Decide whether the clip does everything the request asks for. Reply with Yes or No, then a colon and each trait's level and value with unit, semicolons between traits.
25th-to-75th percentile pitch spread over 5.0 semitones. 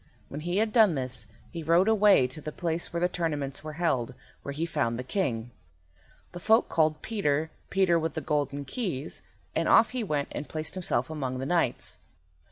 No: average, 4.2 semitones